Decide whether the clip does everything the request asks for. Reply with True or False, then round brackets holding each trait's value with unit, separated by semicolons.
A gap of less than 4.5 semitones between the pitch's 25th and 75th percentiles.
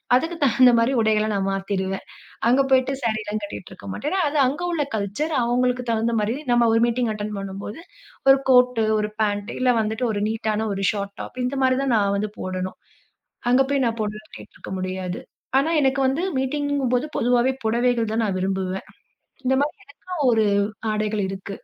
True (4.0 semitones)